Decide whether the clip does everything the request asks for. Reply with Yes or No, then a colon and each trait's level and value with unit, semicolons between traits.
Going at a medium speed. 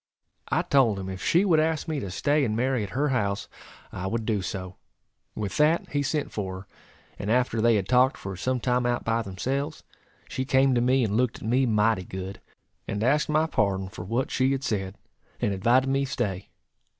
No: fast, 210 wpm